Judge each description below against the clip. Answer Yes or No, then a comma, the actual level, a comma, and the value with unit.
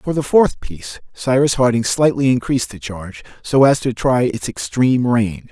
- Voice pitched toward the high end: No, low, 120 Hz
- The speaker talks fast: No, average, 185 wpm